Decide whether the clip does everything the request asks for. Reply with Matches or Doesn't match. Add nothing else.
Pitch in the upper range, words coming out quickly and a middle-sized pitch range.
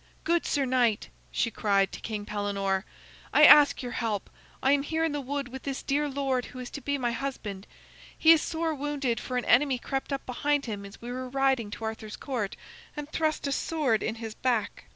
Matches